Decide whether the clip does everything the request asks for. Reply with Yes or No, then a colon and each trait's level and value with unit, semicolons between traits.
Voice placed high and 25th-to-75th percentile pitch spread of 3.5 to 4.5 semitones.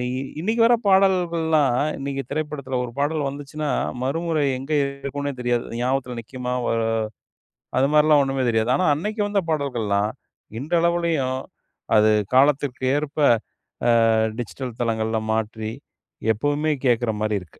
No: medium, 140 Hz; average, 4.2 semitones